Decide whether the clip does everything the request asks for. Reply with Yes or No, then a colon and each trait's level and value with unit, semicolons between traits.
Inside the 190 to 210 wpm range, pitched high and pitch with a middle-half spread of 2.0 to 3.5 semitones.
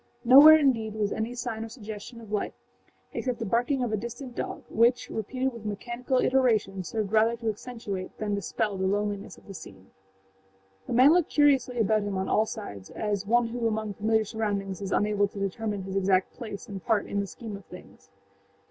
Yes: average, 195 wpm; high, 220 Hz; average, 3.0 semitones